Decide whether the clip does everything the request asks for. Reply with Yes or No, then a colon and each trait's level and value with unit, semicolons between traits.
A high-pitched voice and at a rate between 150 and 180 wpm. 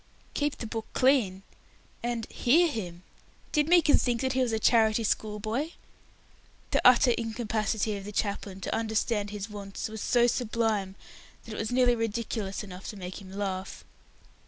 Yes: high, 220 Hz; average, 165 wpm